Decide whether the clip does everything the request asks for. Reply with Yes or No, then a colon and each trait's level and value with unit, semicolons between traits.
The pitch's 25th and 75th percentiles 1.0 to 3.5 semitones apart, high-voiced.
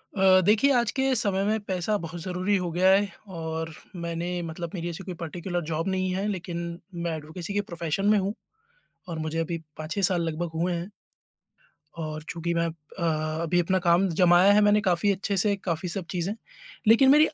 No: average, 2.8 semitones; medium, 175 Hz